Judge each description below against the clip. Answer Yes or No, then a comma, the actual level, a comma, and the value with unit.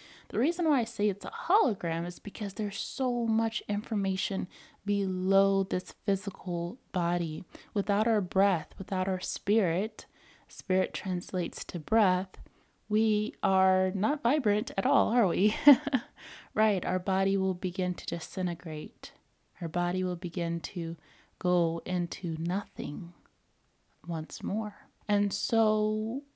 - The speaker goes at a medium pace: No, slow, 125 wpm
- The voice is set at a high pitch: Yes, high, 195 Hz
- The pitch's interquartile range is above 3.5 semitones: No, average, 3.2 semitones